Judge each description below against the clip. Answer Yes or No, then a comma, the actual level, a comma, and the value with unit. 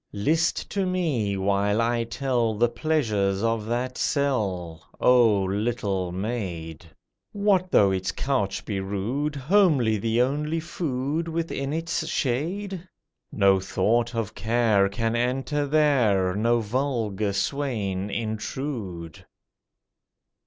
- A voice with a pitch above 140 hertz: No, low, 115 Hz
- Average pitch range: No, wide, 6.0 semitones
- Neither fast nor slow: No, slow, 110 wpm